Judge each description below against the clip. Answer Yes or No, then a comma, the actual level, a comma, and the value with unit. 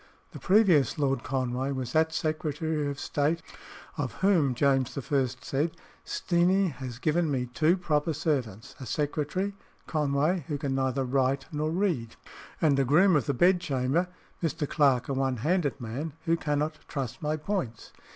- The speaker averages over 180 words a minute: No, average, 155 wpm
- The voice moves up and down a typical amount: Yes, average, 3.5 semitones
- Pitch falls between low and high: Yes, medium, 145 Hz